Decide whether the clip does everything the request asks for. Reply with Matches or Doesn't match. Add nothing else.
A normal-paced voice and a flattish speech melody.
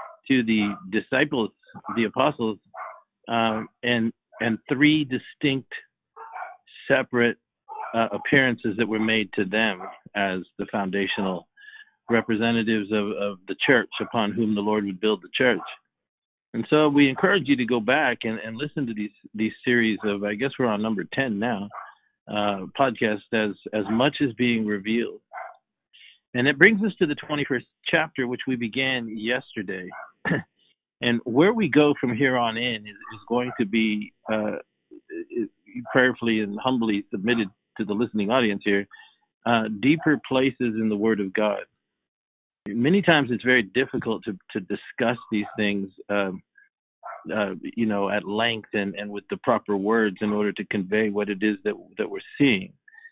Doesn't match